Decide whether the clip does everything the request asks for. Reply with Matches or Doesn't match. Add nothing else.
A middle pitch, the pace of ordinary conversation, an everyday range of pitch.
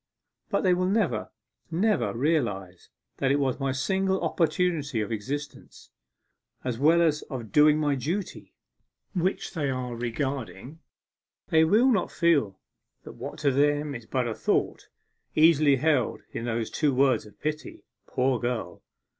Matches